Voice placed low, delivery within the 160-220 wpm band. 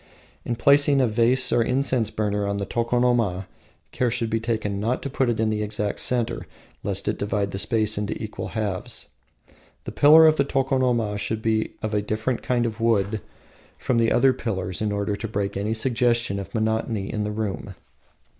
Yes: low, 110 Hz; average, 190 wpm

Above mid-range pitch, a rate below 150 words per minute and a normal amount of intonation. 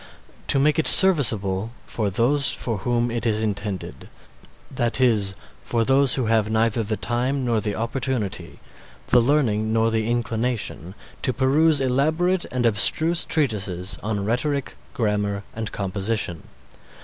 No: low, 115 Hz; slow, 135 wpm; average, 4.0 semitones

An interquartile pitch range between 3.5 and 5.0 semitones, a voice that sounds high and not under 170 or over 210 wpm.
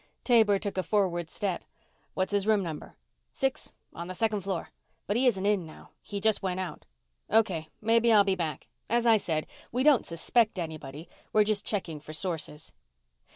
Yes: average, 4.3 semitones; high, 195 Hz; average, 180 wpm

